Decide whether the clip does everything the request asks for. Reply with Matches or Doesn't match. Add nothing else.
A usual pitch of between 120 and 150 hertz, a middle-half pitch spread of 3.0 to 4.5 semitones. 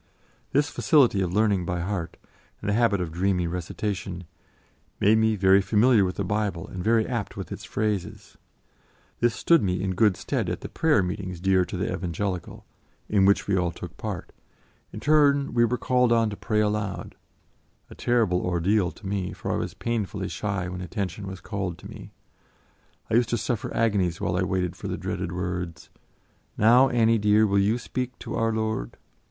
Doesn't match